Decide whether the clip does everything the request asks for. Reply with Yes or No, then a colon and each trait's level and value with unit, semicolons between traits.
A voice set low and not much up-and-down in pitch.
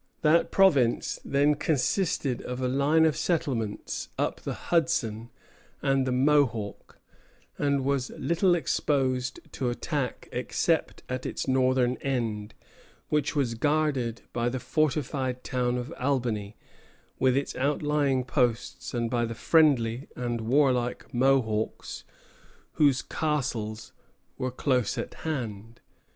No: low, 130 Hz; average, 3.4 semitones